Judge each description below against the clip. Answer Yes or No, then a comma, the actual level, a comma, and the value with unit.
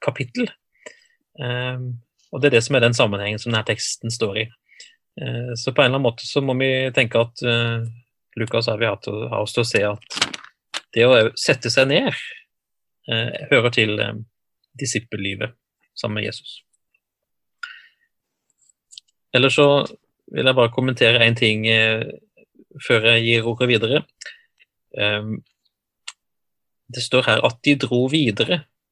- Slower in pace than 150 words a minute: Yes, average, 140 wpm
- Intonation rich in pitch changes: No, average, 3.1 semitones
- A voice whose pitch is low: Yes, low, 120 Hz